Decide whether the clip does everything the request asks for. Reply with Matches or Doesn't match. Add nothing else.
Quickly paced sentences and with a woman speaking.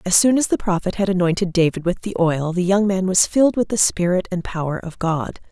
Matches